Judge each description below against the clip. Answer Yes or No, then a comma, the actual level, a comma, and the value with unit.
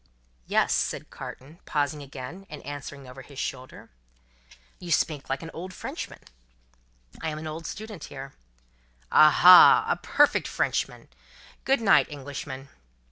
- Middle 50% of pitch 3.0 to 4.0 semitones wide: Yes, average, 3.5 semitones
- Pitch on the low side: No, medium, 145 Hz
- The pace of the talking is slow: Yes, slow, 130 wpm